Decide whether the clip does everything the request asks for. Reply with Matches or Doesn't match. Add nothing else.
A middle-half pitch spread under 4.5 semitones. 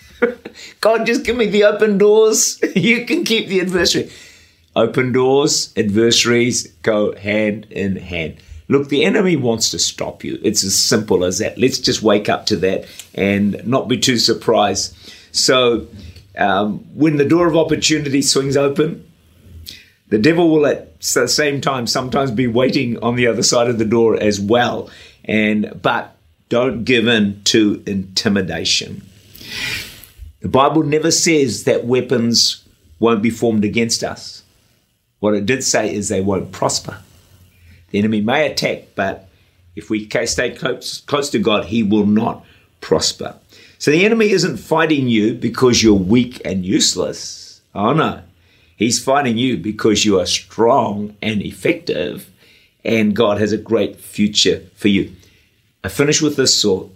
Doesn't match